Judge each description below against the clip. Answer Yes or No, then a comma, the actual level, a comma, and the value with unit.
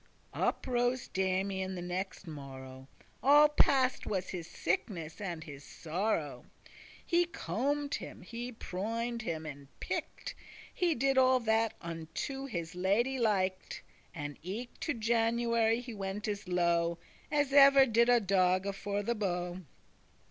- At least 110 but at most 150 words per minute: Yes, average, 140 wpm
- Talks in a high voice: Yes, high, 200 Hz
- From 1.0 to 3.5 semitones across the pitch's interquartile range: No, wide, 5.4 semitones